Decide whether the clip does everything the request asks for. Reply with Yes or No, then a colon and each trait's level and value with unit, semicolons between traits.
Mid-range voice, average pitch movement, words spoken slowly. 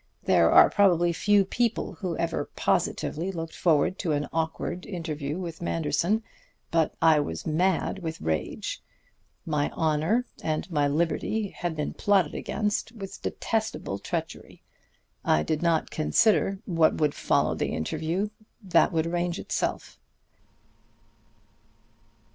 Yes: medium, 165 Hz; average, 3.6 semitones; slow, 125 wpm